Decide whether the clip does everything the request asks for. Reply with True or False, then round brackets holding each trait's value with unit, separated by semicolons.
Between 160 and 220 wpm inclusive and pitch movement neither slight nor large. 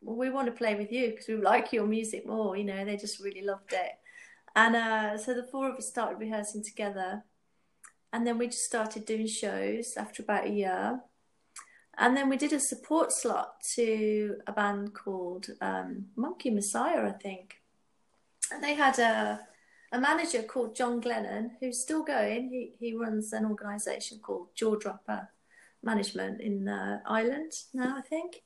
True (175 wpm; 3.2 semitones)